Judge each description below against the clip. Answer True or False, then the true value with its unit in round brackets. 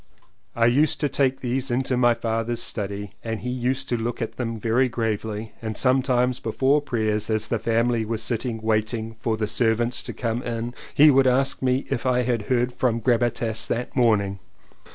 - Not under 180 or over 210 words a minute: True (185 wpm)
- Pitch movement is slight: True (2.1 semitones)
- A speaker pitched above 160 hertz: False (120 Hz)